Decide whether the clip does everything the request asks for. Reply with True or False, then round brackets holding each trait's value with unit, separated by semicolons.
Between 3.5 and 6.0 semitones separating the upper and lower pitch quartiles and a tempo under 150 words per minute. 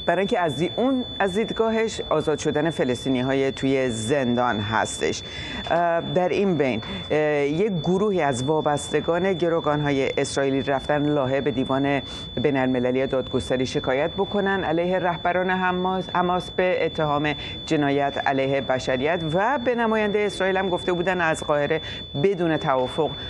True (5.3 semitones; 125 wpm)